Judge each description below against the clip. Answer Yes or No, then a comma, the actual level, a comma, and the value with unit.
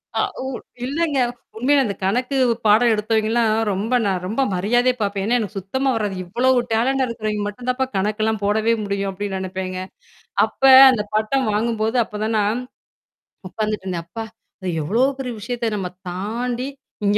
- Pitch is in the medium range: No, high, 220 Hz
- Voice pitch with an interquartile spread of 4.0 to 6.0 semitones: No, average, 3.4 semitones